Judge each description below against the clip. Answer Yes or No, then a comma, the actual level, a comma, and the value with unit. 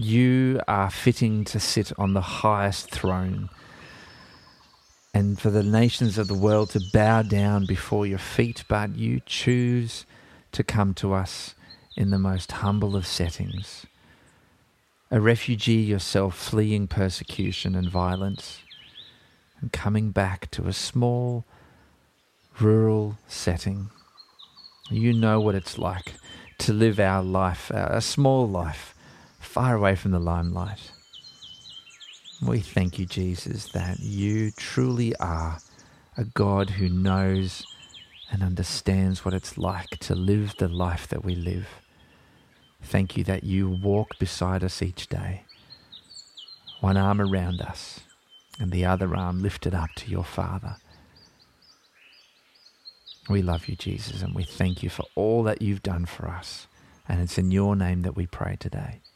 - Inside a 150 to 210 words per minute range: No, average, 140 wpm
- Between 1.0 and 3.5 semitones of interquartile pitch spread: Yes, average, 2.8 semitones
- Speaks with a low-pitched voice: Yes, very low, 95 Hz